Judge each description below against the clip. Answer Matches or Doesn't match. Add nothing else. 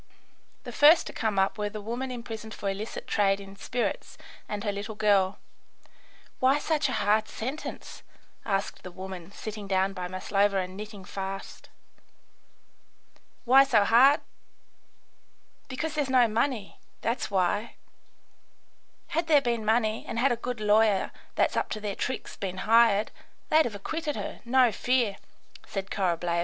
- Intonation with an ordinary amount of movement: Matches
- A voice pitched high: Matches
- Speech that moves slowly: Doesn't match